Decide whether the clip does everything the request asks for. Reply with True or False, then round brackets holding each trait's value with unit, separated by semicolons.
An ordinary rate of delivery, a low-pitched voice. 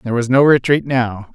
False (220 wpm; 125 Hz)